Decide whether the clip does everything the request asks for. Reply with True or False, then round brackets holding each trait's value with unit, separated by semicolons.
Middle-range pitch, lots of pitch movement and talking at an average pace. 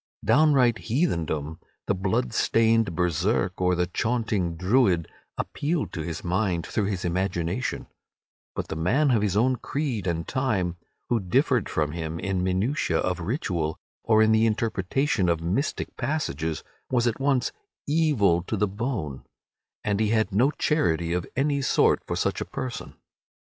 False (100 Hz; 6.2 semitones; 155 wpm)